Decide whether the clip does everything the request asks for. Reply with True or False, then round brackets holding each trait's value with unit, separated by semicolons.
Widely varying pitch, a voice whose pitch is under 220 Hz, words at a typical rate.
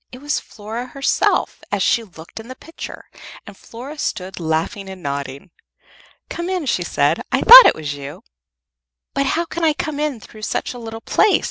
False (8.2 semitones; 230 Hz; 190 wpm)